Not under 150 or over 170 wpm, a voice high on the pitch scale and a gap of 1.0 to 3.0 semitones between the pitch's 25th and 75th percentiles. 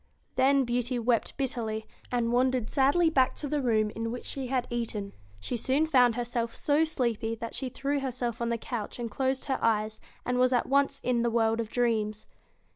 No: average, 200 wpm; high, 245 Hz; narrow, 2.6 semitones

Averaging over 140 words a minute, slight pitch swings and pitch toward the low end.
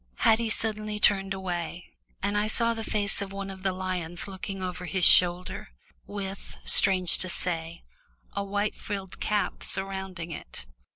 No: average, 155 wpm; narrow, 2.1 semitones; high, 195 Hz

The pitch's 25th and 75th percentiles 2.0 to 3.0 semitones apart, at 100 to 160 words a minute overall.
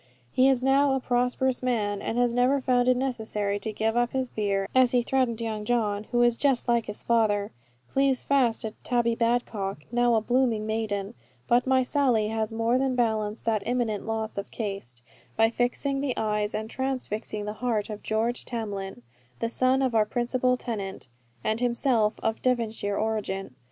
No: average, 2.7 semitones; average, 180 wpm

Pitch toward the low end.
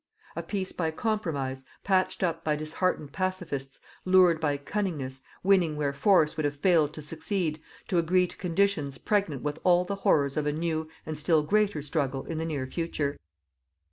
No: medium, 160 Hz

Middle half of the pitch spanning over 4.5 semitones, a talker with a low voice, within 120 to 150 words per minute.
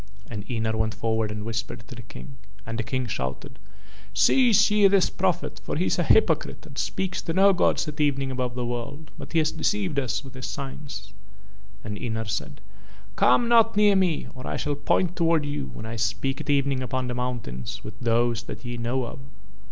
No: wide, 5.6 semitones; low, 130 Hz; average, 200 wpm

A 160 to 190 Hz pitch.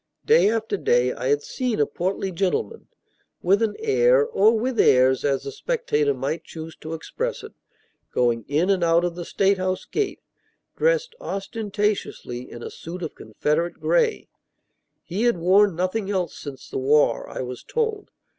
Yes: medium, 185 Hz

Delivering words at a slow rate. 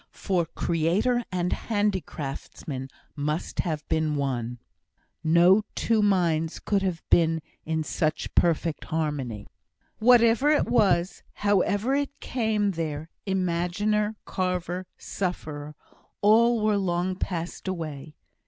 Yes: slow, 105 wpm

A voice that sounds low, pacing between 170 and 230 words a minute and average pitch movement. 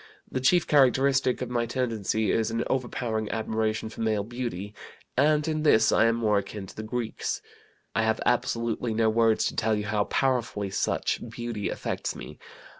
No: low, 115 Hz; average, 175 wpm; narrow, 2.3 semitones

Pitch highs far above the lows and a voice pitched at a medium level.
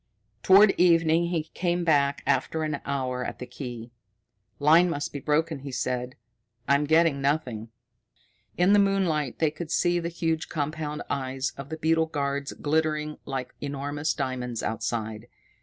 No: average, 3.3 semitones; medium, 150 Hz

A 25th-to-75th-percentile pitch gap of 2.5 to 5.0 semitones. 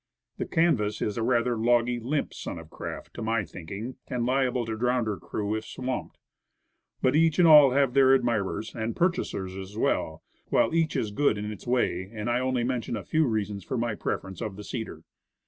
Yes: average, 3.5 semitones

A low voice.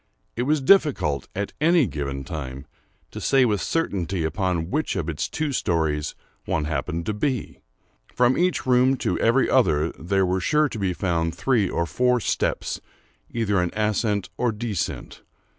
Yes: low, 100 Hz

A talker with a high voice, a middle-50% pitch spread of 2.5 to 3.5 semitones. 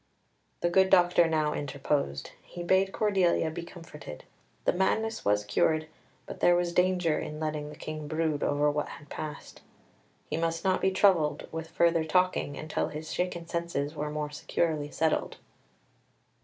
No: medium, 160 Hz; average, 2.9 semitones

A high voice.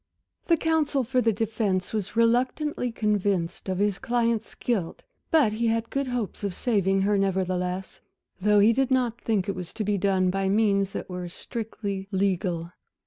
Yes: high, 210 Hz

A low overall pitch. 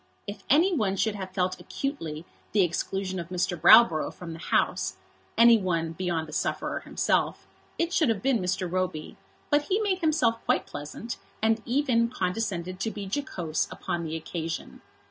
No: high, 190 Hz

